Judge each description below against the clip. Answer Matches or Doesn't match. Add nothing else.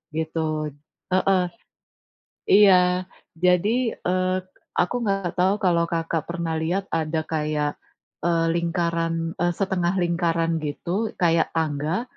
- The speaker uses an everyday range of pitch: Doesn't match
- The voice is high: Doesn't match